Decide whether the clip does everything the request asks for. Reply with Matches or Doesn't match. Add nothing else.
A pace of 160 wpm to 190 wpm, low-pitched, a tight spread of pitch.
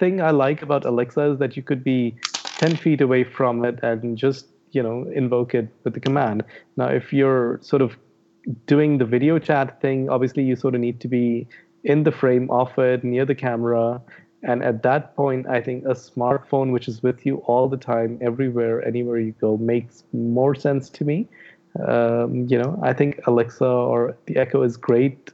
Doesn't match